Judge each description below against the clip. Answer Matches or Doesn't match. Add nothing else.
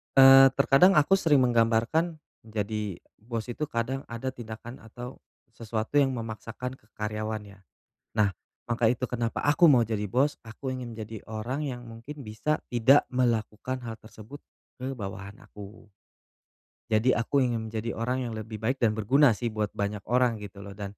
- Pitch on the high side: Doesn't match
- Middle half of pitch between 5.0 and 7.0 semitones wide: Doesn't match